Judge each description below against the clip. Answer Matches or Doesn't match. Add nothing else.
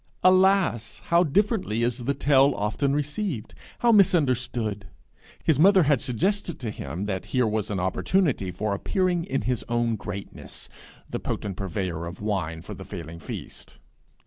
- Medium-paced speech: Matches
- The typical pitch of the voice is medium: Doesn't match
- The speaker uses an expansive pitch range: Matches